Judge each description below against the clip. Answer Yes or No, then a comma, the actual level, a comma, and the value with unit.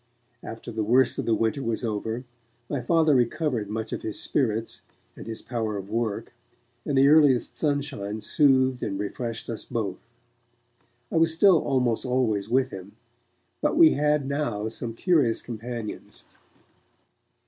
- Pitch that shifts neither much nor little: Yes, average, 4.2 semitones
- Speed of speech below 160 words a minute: Yes, average, 150 wpm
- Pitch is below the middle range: Yes, low, 120 Hz